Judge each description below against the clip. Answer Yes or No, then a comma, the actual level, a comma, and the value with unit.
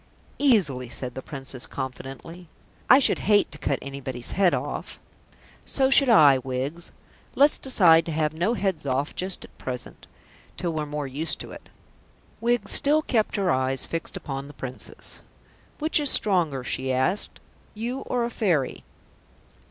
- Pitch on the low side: No, medium, 160 Hz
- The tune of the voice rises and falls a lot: Yes, wide, 7.9 semitones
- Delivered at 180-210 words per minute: No, average, 155 wpm